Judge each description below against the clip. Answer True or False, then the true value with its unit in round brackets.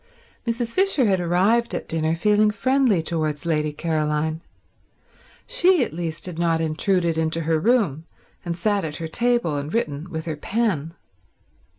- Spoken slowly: False (155 wpm)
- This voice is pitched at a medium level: True (170 Hz)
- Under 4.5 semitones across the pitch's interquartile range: False (5.5 semitones)